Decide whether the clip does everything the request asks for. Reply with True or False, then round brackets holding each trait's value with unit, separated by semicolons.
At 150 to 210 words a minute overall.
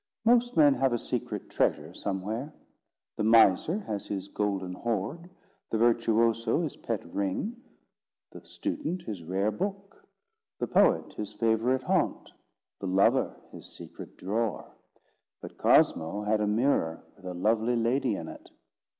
False (140 wpm)